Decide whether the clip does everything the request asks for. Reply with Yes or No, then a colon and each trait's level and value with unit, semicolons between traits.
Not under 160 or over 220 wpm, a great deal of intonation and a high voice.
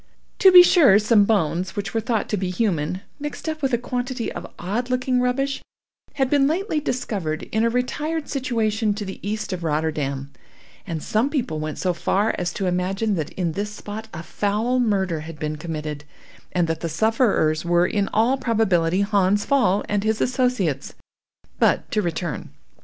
Yes: average, 180 wpm; wide, 6.2 semitones; high, 205 Hz